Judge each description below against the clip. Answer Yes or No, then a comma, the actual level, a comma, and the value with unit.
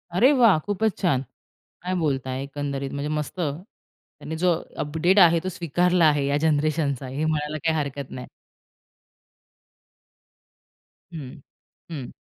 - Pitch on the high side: No, medium, 155 Hz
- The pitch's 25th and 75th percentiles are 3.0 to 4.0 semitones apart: Yes, average, 3.7 semitones